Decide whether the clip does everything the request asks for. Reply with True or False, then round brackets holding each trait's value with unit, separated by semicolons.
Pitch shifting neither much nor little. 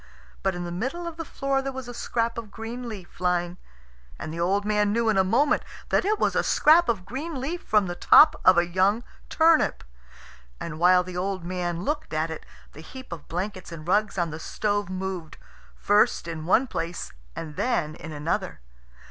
False (5.9 semitones)